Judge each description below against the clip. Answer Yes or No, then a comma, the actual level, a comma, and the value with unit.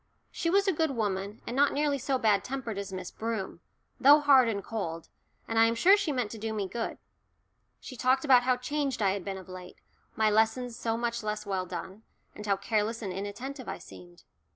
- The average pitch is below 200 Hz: No, high, 225 Hz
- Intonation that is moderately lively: Yes, average, 4.6 semitones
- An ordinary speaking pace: No, fast, 215 wpm